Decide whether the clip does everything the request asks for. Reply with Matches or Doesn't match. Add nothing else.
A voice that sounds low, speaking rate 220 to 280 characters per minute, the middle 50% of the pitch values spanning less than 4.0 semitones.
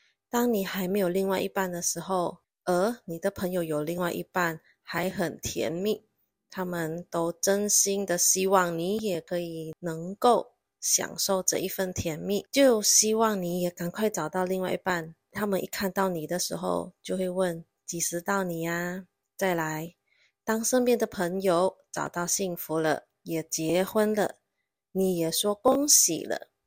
Doesn't match